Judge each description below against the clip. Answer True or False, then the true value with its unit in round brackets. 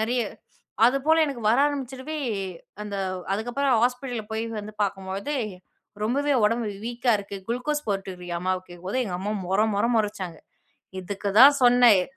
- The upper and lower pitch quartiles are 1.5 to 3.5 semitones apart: False (4.7 semitones)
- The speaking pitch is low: False (225 Hz)